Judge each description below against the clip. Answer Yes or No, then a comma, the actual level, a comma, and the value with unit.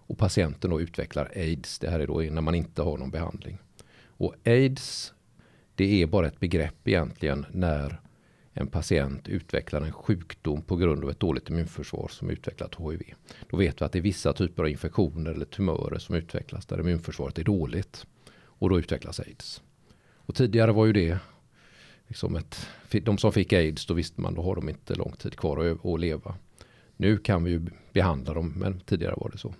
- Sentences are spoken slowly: No, average, 190 wpm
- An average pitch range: Yes, average, 4.0 semitones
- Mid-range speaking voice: No, very low, 85 Hz